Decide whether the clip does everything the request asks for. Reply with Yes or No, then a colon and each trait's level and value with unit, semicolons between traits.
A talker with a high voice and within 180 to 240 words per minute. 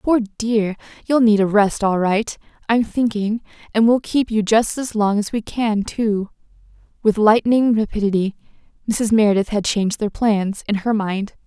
No: high, 215 Hz; average, 165 wpm